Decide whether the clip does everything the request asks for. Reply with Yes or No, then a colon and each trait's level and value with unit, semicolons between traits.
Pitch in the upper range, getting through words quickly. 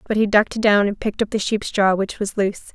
Yes: high, 205 Hz; fast, 285 wpm